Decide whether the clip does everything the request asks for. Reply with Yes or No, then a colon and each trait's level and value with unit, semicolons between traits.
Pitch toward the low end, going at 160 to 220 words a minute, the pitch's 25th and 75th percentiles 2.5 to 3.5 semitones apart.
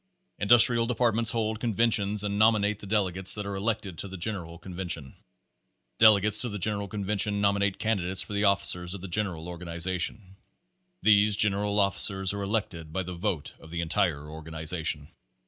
Yes: low, 100 Hz; average, 170 wpm; average, 3.2 semitones